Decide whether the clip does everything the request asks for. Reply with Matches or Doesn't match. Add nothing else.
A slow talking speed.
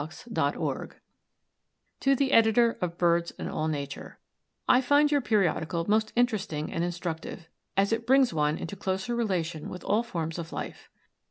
Doesn't match